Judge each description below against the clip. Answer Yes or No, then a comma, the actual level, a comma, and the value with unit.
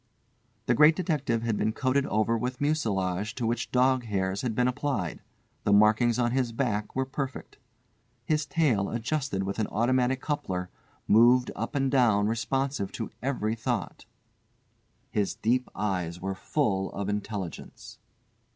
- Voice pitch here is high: No, low, 115 Hz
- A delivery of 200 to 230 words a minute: No, average, 145 wpm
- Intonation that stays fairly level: No, average, 4.3 semitones